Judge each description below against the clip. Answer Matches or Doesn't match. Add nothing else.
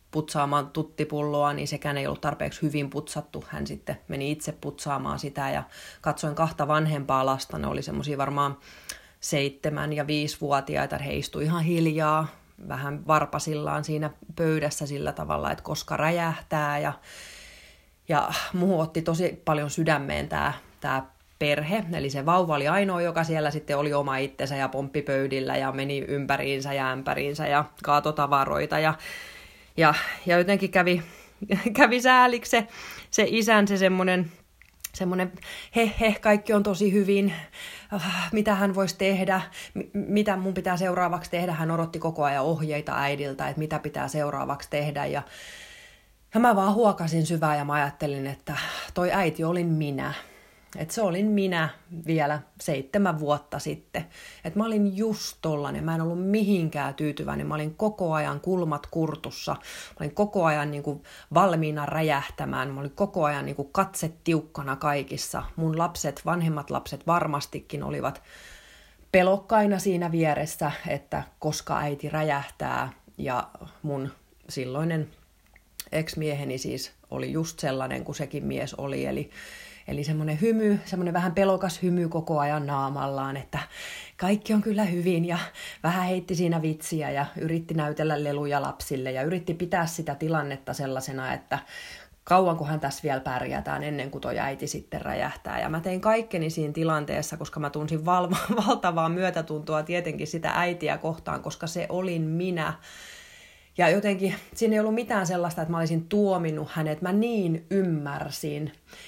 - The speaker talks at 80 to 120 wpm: Doesn't match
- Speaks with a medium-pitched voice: Matches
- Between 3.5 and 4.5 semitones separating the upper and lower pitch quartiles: Matches